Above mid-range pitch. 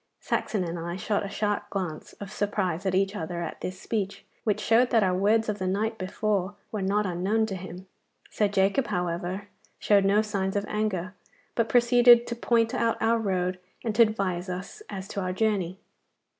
Yes: high, 200 Hz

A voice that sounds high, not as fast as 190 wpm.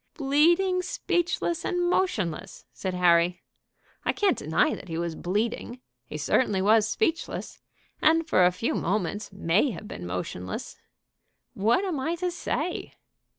Yes: high, 220 Hz; average, 140 wpm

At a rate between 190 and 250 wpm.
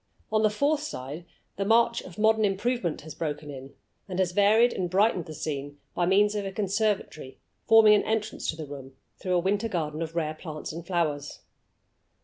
Yes: average, 195 wpm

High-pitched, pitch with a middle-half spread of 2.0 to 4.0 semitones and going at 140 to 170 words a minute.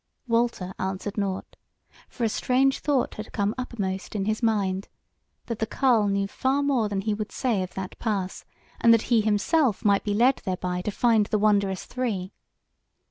No: high, 210 Hz; average, 3.4 semitones; average, 180 wpm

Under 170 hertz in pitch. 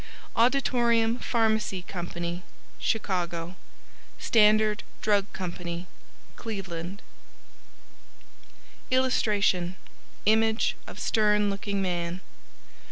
No: high, 205 Hz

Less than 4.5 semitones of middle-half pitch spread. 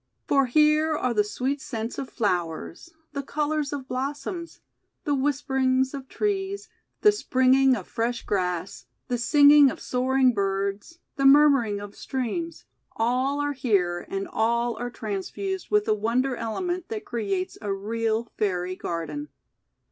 No: wide, 5.5 semitones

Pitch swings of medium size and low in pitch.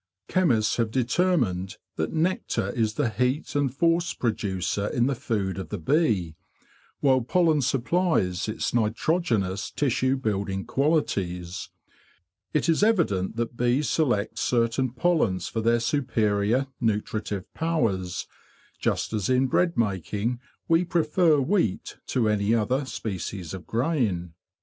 No: wide, 6.4 semitones; low, 120 Hz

